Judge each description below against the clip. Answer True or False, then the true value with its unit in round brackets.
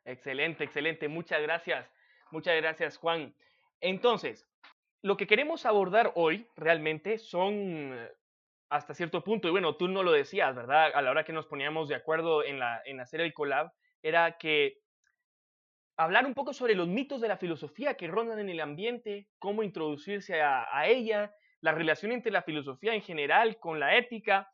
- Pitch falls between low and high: True (180 Hz)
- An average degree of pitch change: False (6.0 semitones)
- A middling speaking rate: True (170 wpm)